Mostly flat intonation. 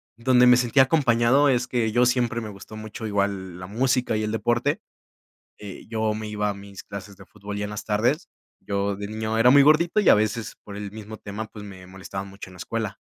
No: average, 3.3 semitones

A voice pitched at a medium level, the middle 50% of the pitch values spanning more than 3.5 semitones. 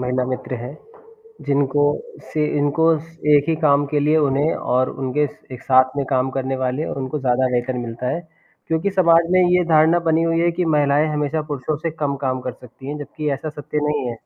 No: medium, 145 Hz; average, 3.2 semitones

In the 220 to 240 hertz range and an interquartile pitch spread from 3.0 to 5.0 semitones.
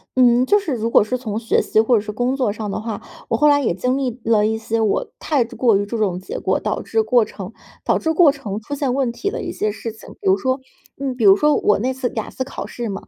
Yes: high, 235 Hz; average, 3.6 semitones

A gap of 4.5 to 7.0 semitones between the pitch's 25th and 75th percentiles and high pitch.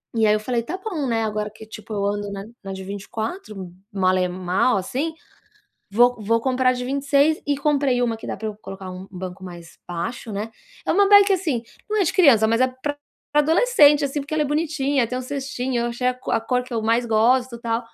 Yes: average, 5.0 semitones; high, 240 Hz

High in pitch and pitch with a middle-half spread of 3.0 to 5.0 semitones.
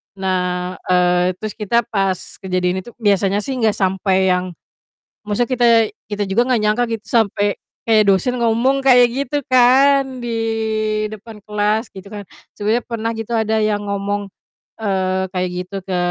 Yes: high, 210 Hz; average, 3.7 semitones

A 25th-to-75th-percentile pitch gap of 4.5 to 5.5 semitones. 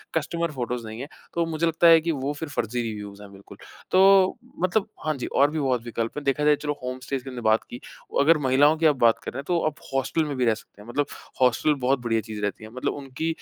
Yes: average, 4.8 semitones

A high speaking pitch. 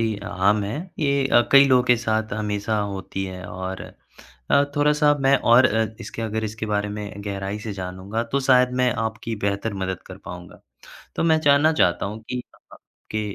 No: low, 110 Hz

